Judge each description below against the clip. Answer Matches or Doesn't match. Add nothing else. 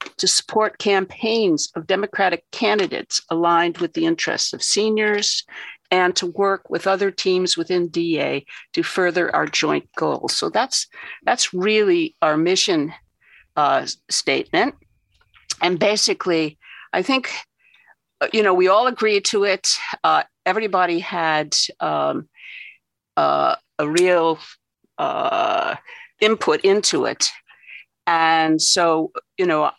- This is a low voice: Doesn't match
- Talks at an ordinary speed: Doesn't match